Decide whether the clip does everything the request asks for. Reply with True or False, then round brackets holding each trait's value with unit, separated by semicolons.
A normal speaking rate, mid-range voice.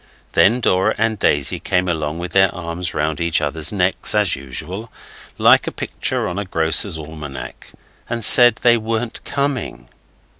False (155 wpm; 90 Hz)